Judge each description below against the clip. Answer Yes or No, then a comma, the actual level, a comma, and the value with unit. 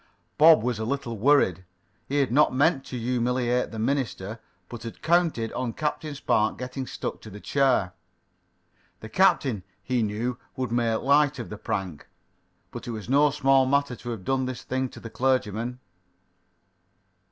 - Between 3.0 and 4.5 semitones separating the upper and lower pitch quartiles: Yes, average, 3.4 semitones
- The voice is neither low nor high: No, low, 125 Hz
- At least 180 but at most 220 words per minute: No, average, 165 wpm